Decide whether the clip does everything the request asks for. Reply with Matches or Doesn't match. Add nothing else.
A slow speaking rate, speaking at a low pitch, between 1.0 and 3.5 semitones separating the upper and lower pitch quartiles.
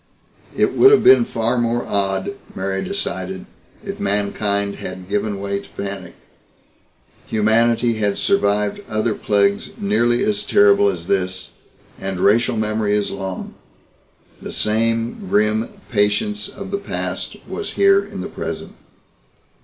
Matches